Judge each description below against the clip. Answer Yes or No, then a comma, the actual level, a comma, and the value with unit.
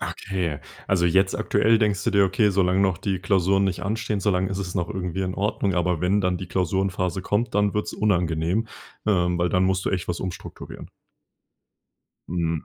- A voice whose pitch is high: No, very low, 95 Hz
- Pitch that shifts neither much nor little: No, narrow, 2.0 semitones